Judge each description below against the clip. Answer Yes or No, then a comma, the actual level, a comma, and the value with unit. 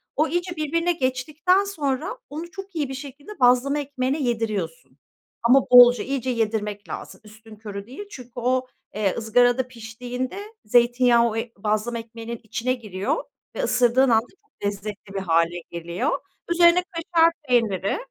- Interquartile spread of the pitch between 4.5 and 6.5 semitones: Yes, average, 4.8 semitones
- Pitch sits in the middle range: No, high, 245 Hz